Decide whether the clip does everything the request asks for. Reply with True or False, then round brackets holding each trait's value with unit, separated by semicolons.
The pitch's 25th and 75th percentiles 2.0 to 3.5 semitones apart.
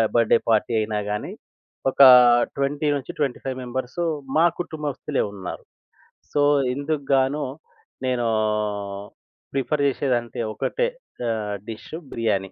False (4.0 semitones)